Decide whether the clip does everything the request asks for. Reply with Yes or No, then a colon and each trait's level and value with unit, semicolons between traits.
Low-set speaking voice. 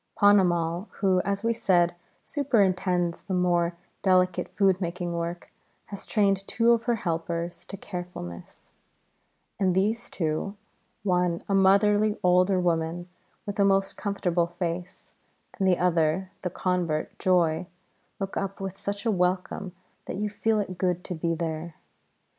No: medium, 185 Hz